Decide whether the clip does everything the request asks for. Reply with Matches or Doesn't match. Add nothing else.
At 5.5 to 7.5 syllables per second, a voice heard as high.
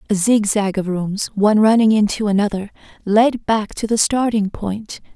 Doesn't match